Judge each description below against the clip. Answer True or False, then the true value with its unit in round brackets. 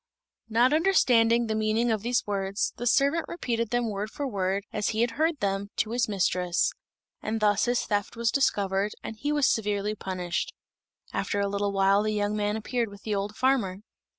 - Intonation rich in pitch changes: False (3.0 semitones)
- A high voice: True (215 Hz)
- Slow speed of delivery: False (190 wpm)